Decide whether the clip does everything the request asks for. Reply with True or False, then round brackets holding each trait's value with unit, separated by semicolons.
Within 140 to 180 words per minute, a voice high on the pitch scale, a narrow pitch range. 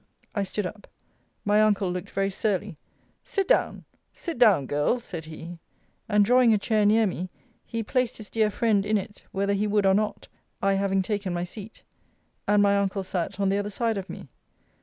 False (195 wpm; 205 Hz; 1.9 semitones)